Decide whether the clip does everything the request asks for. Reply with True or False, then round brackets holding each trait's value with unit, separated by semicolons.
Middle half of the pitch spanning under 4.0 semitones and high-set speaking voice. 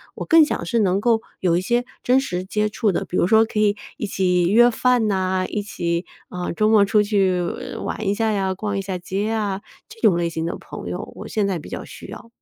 True (3.1 semitones; 200 Hz)